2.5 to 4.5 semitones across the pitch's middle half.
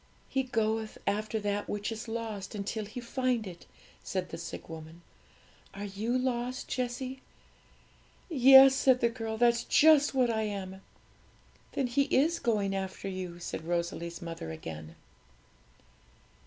No: average, 4.9 semitones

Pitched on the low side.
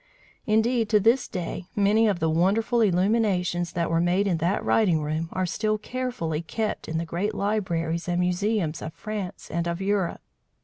No: medium, 185 Hz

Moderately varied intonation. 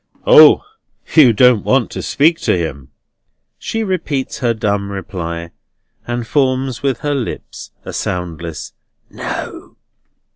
No: wide, 7.6 semitones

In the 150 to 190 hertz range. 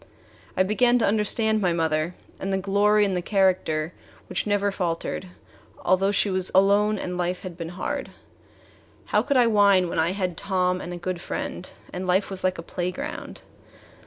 Yes: medium, 185 Hz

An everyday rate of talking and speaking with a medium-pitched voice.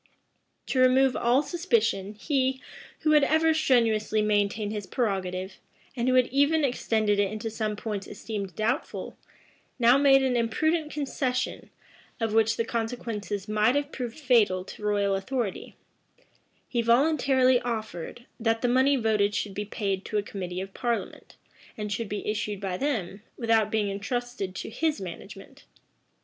No: average, 150 wpm; high, 225 Hz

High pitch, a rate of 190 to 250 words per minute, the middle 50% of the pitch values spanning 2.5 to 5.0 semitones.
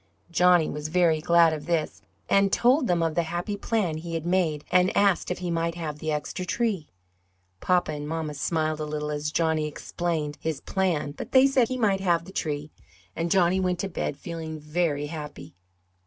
No: medium, 165 Hz; average, 195 wpm; average, 3.0 semitones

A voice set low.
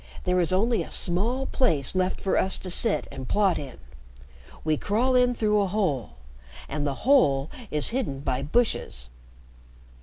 No: medium, 185 Hz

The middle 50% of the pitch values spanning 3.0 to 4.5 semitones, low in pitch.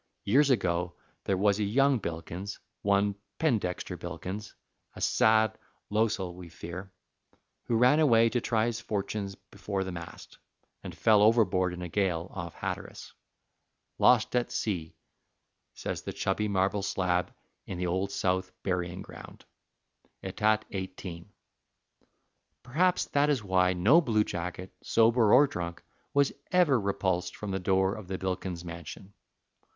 Yes: average, 3.5 semitones; low, 100 Hz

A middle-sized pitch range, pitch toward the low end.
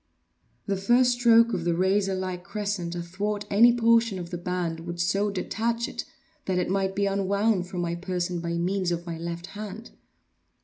No: average, 3.0 semitones; high, 190 Hz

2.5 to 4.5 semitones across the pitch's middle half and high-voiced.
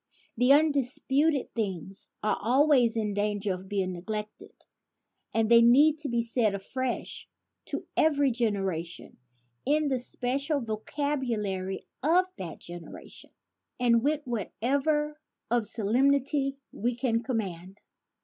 No: average, 5.2 semitones; high, 235 Hz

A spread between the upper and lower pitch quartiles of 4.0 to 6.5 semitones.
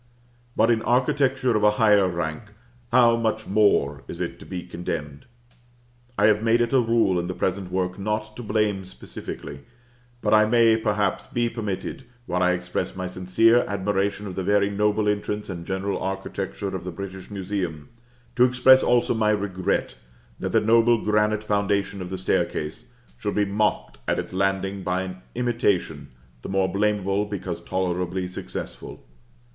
No: average, 2.7 semitones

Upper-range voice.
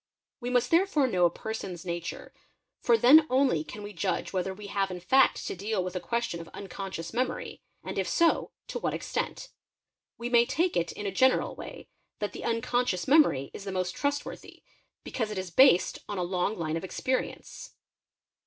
Yes: high, 210 Hz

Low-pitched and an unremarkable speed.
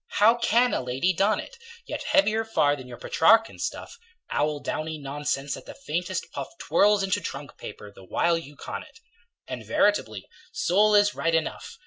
No: medium, 170 Hz; average, 175 wpm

